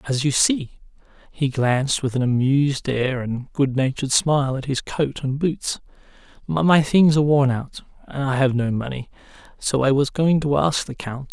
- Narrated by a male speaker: Yes, male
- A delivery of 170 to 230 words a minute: Yes, average, 185 wpm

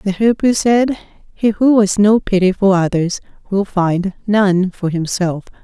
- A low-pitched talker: No, high, 195 Hz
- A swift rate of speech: No, average, 160 wpm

